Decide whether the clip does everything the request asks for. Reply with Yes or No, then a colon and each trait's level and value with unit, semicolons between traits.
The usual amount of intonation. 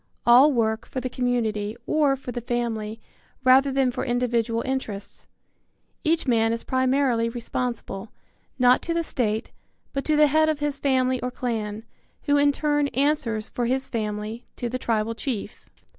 Yes: average, 3.1 semitones